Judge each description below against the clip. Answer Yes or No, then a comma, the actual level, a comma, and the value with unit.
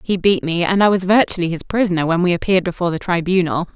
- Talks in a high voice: No, medium, 180 Hz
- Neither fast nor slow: No, fast, 240 wpm